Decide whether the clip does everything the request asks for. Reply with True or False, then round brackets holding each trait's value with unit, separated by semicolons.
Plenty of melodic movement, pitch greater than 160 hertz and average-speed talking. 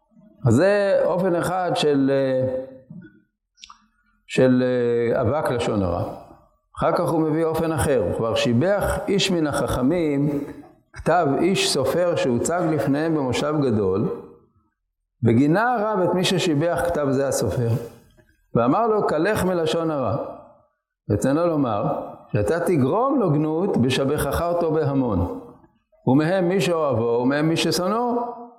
False (5.7 semitones; 150 Hz; 120 wpm)